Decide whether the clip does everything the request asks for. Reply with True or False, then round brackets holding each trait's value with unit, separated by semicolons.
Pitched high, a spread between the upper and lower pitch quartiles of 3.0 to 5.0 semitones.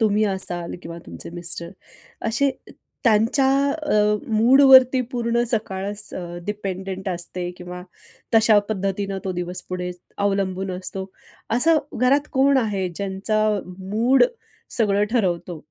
True (200 Hz; 3.9 semitones)